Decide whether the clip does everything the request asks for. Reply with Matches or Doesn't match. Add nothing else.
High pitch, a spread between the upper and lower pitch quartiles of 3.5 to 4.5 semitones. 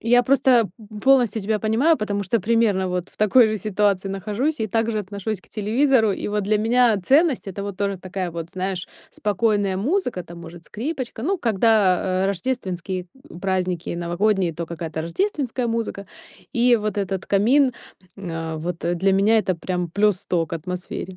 Matches